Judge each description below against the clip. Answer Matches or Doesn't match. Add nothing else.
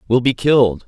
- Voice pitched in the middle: Doesn't match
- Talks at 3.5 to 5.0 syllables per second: Doesn't match